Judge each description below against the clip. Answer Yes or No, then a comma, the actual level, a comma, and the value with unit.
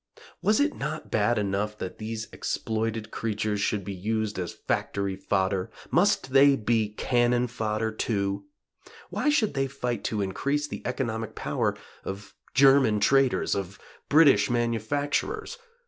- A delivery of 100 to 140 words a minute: Yes, slow, 135 wpm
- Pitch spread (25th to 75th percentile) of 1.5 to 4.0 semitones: No, average, 4.7 semitones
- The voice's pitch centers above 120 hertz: No, low, 115 Hz